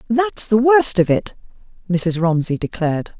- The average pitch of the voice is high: Yes, high, 205 Hz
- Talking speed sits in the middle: Yes, average, 150 wpm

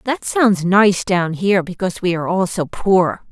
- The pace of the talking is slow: No, average, 200 wpm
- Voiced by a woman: Yes, female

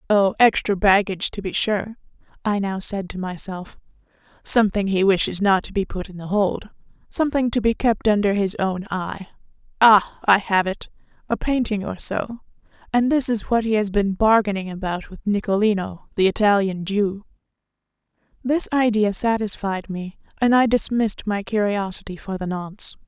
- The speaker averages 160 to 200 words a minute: No, average, 150 wpm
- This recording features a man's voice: No, female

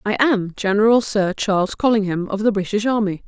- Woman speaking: Yes, female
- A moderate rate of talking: Yes, average, 185 wpm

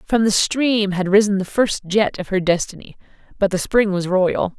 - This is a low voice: No, high, 200 Hz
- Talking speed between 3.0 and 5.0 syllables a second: Yes, 4.7 syllables/s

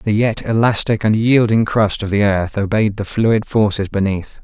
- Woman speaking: No, male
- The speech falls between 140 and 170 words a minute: No, average, 190 wpm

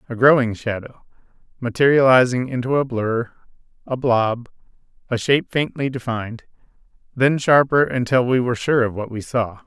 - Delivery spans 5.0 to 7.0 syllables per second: Yes, 5.2 syllables/s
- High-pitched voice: No, low, 125 Hz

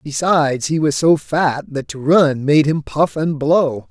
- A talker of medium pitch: Yes, medium, 145 Hz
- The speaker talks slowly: No, average, 200 wpm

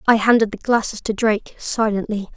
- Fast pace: No, average, 180 wpm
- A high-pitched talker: Yes, high, 215 Hz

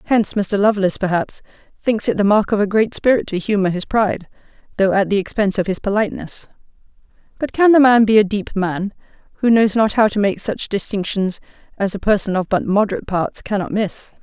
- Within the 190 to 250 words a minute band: Yes, average, 200 wpm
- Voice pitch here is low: No, high, 205 Hz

